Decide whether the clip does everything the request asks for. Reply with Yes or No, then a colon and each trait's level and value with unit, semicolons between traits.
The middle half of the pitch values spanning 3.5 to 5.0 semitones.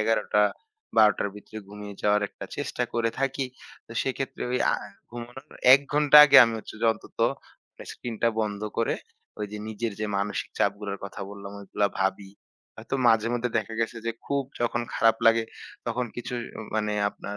No: narrow, 2.6 semitones